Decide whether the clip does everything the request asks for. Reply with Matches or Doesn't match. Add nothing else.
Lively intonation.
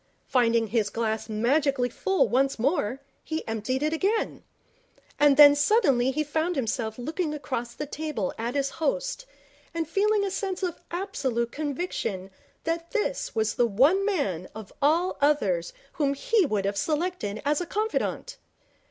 Matches